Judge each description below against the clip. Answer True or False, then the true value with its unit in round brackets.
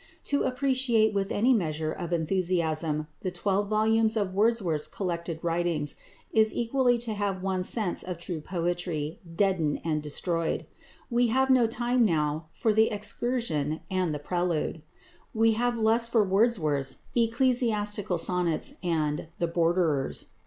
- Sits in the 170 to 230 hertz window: True (190 Hz)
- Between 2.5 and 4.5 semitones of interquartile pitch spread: False (5.3 semitones)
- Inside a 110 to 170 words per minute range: True (140 wpm)